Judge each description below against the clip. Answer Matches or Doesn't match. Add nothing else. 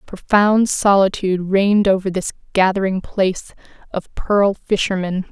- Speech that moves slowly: Matches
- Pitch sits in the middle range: Doesn't match